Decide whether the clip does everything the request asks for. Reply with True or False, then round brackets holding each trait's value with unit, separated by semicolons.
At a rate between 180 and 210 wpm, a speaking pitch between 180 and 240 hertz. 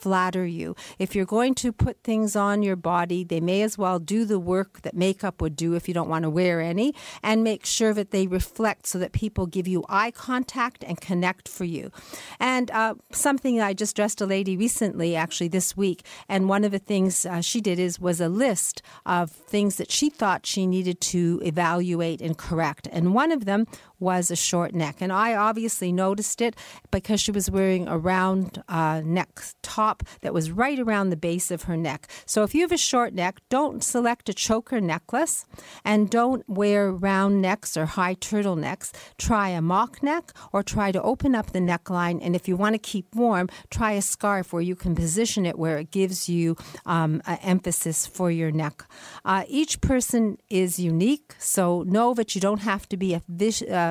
True (205 wpm; 190 Hz)